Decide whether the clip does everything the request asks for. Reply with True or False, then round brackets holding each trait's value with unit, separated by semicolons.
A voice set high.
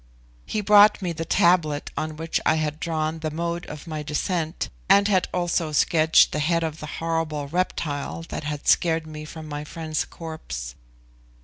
False (160 Hz)